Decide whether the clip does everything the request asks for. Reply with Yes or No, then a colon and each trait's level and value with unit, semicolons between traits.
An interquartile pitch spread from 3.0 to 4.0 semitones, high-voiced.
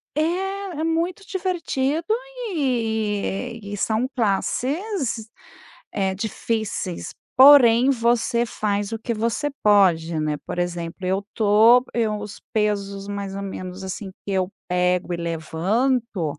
No: average, 4.4 semitones; high, 210 Hz